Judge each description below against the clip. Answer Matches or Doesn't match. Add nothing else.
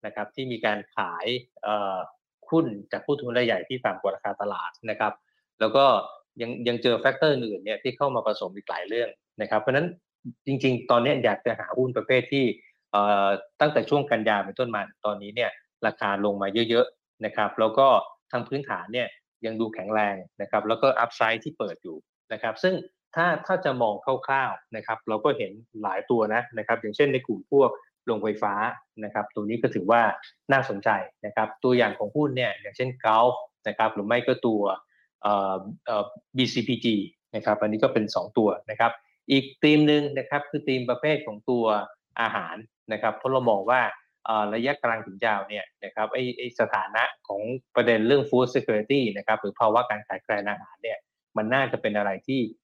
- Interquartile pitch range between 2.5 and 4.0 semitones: Matches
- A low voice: Matches